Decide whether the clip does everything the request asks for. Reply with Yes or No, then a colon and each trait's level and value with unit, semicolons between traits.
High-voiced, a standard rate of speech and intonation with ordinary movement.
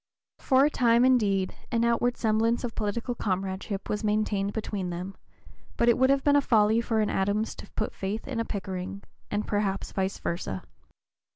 Yes: high, 215 Hz; average, 175 wpm; average, 3.1 semitones